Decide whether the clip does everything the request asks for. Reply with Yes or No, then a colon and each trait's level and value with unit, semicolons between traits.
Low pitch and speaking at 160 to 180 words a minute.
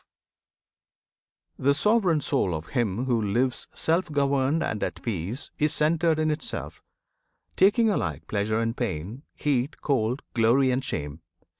No: low, 130 Hz; average, 140 wpm